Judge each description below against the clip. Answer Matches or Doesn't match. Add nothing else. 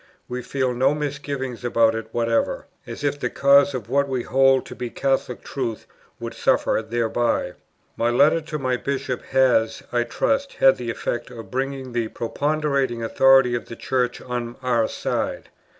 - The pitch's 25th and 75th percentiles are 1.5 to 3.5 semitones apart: Matches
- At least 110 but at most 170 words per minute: Matches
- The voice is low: Matches